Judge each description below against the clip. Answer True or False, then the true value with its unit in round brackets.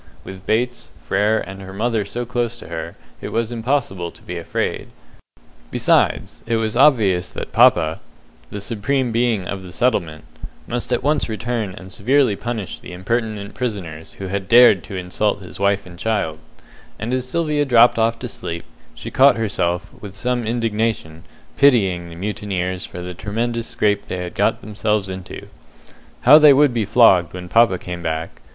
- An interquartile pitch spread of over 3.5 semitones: True (4.4 semitones)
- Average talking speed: True (170 wpm)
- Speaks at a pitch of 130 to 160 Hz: False (105 Hz)